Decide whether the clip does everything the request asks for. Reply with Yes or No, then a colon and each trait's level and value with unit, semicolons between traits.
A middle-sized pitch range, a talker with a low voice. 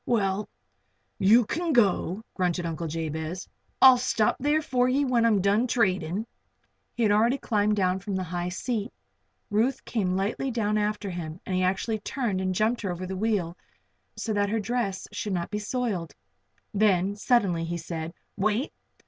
No: average, 4.0 semitones; high, 205 Hz